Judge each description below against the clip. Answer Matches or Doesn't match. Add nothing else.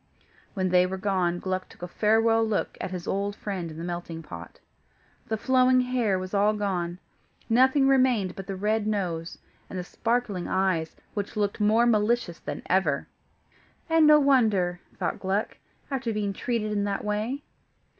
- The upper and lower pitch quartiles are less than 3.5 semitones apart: Doesn't match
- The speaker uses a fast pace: Doesn't match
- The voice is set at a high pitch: Matches